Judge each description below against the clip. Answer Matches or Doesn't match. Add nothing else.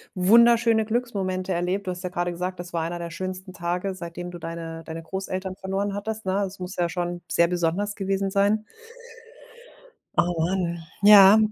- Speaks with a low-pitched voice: Doesn't match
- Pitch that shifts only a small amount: Matches